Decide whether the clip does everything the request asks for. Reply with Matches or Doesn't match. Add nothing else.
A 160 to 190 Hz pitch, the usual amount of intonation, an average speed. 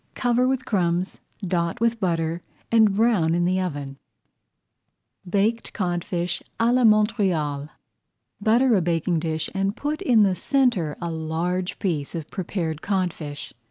Matches